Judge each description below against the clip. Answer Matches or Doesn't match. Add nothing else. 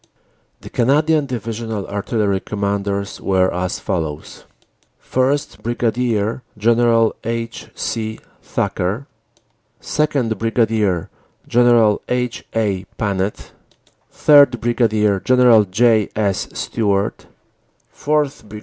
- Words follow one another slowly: Matches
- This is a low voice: Matches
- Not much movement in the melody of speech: Doesn't match